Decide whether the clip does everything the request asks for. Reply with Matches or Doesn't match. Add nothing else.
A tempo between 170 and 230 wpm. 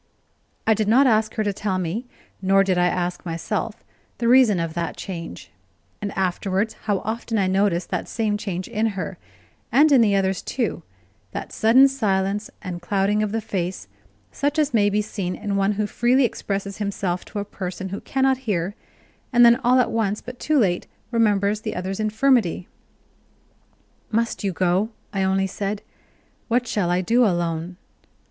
Matches